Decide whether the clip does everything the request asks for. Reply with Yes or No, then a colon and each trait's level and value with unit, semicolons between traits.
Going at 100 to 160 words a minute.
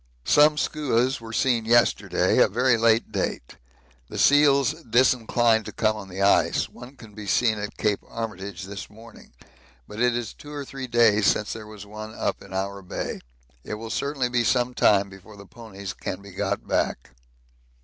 No: average, 180 wpm